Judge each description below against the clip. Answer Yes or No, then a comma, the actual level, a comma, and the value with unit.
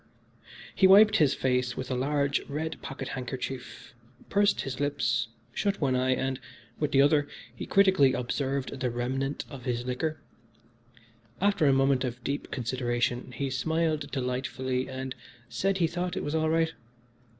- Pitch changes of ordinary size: Yes, average, 3.7 semitones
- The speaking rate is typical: Yes, average, 160 wpm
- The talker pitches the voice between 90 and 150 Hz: Yes, low, 135 Hz